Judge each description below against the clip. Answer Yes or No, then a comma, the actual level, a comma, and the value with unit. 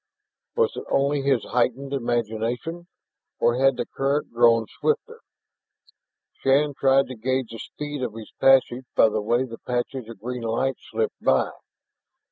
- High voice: No, low, 125 Hz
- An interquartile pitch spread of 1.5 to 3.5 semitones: Yes, average, 2.8 semitones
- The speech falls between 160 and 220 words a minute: No, average, 150 wpm